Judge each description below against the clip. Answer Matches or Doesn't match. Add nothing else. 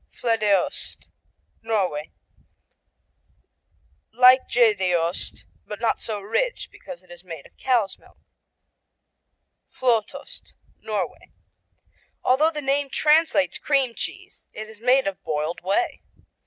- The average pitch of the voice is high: Matches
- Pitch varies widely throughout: Matches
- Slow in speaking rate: Matches